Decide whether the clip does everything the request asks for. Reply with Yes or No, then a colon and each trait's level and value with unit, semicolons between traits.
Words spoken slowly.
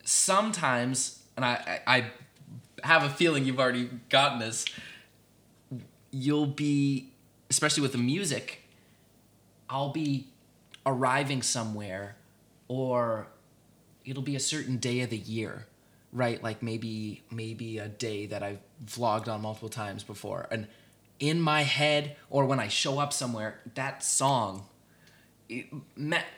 Yes: slow, 130 wpm